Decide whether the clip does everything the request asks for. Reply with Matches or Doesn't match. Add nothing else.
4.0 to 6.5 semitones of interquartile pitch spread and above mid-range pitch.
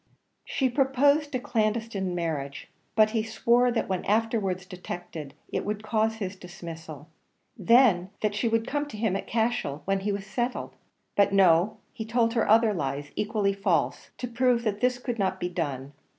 Matches